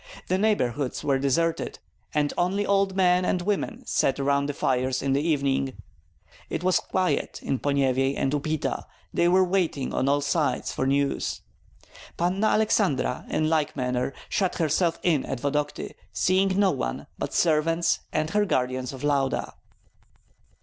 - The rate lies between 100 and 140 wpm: No, average, 150 wpm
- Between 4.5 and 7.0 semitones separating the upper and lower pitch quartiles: Yes, average, 5.0 semitones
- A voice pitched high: No, medium, 150 Hz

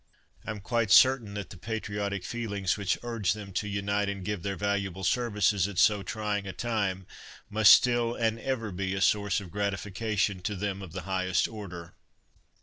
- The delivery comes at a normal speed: Yes, average, 180 wpm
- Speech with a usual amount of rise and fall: No, narrow, 2.1 semitones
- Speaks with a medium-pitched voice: No, low, 100 Hz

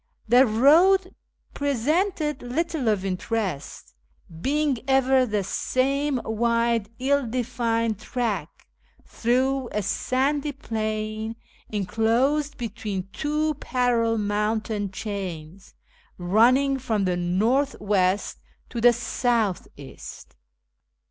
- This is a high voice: Yes, high, 230 Hz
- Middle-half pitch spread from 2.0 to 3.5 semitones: No, average, 4.2 semitones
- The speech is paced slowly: Yes, slow, 95 wpm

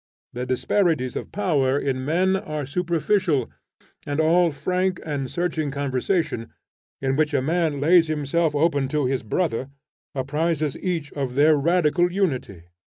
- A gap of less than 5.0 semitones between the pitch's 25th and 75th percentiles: Yes, average, 4.1 semitones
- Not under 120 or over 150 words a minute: Yes, average, 140 wpm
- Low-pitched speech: No, medium, 150 Hz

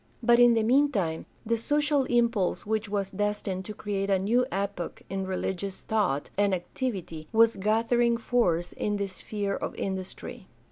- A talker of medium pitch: No, high, 205 Hz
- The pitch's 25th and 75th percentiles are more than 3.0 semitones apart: Yes, average, 3.4 semitones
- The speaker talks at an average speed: Yes, average, 155 wpm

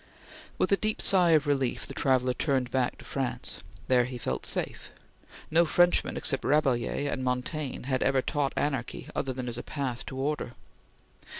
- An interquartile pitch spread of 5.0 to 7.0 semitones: No, average, 2.8 semitones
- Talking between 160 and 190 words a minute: Yes, average, 170 wpm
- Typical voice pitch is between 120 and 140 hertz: Yes, low, 135 Hz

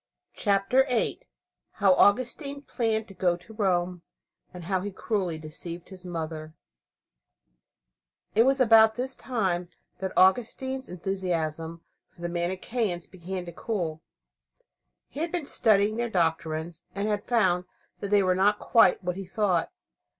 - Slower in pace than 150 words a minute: Yes, average, 140 wpm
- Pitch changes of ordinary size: Yes, average, 4.2 semitones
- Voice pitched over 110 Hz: Yes, high, 190 Hz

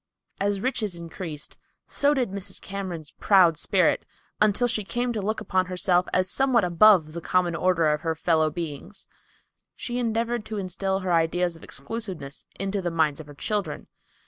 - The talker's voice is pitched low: No, medium, 185 Hz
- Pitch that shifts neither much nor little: Yes, average, 4.2 semitones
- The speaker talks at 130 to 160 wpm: No, average, 170 wpm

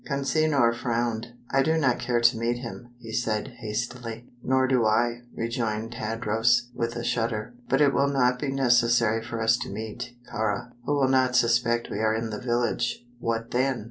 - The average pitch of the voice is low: Yes, low, 120 Hz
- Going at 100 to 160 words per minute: No, average, 180 wpm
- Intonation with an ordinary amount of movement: No, narrow, 1.8 semitones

